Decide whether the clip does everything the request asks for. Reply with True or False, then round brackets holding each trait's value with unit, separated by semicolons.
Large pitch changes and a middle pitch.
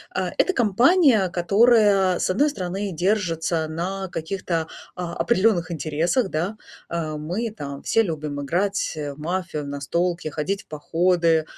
False (4.0 semitones; 175 Hz)